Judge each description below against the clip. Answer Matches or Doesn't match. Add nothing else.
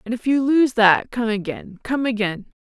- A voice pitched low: Doesn't match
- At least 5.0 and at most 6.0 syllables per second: Doesn't match